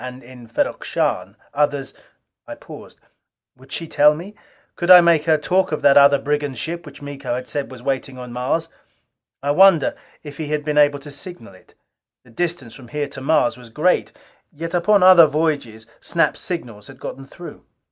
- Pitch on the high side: No, medium, 145 Hz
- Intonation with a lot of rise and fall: No, average, 4.1 semitones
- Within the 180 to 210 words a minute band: Yes, average, 190 wpm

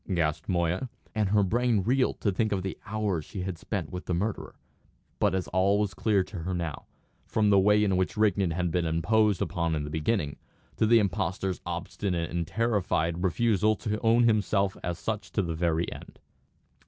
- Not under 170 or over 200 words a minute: Yes, average, 190 wpm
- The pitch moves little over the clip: No, average, 3.8 semitones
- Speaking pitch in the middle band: No, very low, 95 Hz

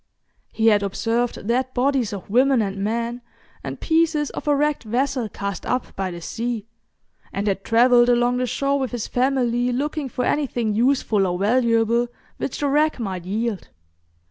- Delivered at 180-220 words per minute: No, average, 170 wpm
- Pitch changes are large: No, average, 3.6 semitones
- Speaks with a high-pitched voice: Yes, high, 240 Hz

